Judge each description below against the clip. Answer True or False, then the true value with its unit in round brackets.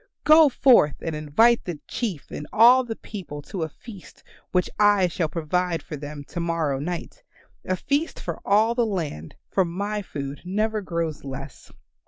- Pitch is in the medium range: True (180 Hz)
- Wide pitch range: True (5.9 semitones)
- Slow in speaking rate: False (170 wpm)